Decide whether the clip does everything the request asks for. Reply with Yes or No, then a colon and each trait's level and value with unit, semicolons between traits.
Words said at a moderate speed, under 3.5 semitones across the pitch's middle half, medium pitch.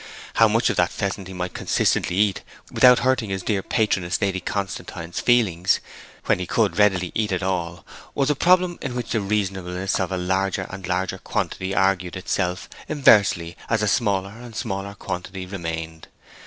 No: average, 170 wpm; average, 2.8 semitones; very low, 95 Hz